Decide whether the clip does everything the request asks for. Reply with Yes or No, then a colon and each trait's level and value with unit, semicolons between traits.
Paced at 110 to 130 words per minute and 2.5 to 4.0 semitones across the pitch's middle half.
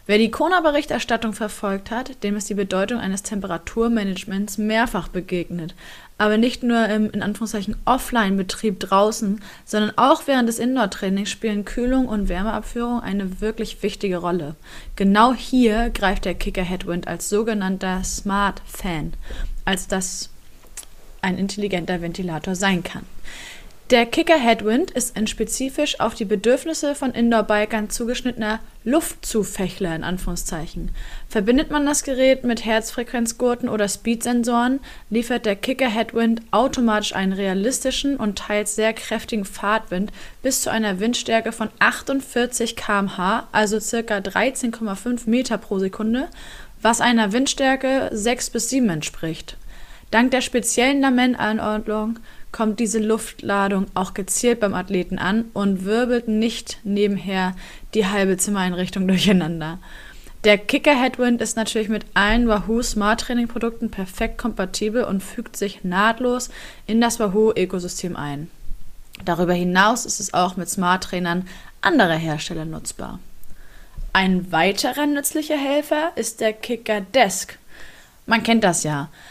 Yes: slow, 125 wpm; average, 3.6 semitones